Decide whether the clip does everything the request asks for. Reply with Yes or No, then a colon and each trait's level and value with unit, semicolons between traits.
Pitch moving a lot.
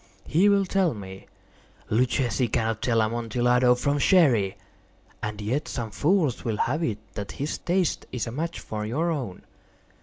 Yes: wide, 5.8 semitones